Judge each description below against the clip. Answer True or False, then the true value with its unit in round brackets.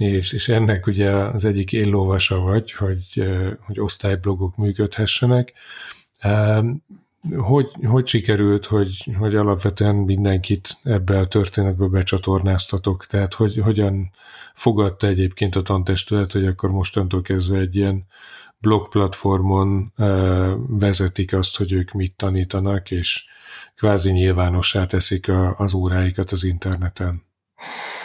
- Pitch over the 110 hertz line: False (100 Hz)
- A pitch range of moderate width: False (1.8 semitones)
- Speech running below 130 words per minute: True (110 wpm)